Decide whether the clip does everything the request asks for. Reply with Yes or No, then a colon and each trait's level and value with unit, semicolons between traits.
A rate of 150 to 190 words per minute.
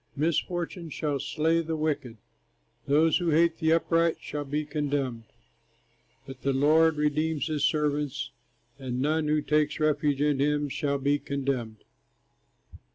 No: slow, 135 wpm